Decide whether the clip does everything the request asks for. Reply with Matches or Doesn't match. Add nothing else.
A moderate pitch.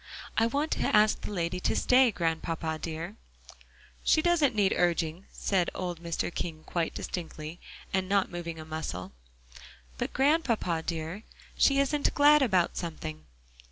Matches